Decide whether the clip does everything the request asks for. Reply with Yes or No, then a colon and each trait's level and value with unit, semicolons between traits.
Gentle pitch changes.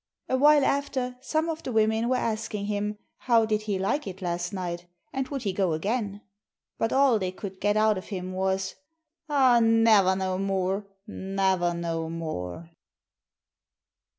No: average, 3.9 semitones